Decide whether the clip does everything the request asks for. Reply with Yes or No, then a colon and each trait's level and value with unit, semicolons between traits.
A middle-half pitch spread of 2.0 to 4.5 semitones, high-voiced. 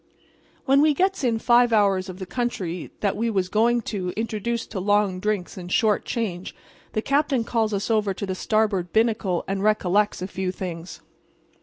Yes: average, 3.6 semitones; high, 210 Hz